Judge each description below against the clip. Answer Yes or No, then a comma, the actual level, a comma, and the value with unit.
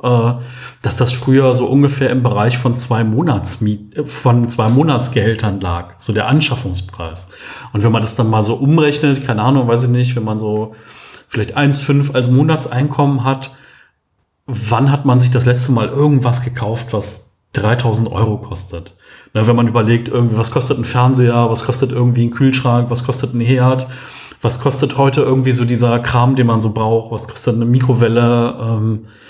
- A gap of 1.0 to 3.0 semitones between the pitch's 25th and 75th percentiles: Yes, narrow, 2.6 semitones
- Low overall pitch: Yes, low, 120 Hz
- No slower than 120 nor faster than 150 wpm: No, average, 175 wpm